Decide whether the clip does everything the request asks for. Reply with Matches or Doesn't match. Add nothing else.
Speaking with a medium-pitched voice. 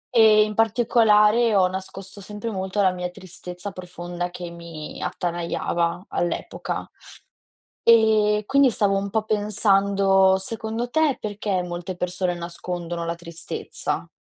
Doesn't match